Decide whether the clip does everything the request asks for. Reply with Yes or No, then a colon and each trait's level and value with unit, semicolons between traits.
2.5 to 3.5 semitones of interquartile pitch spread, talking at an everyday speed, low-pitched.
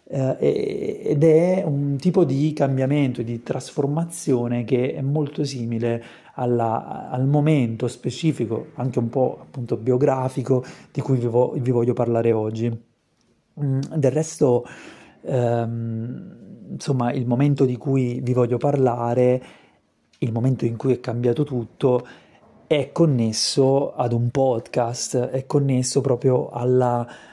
Yes: average, 3.1 semitones; average, 125 wpm; low, 130 Hz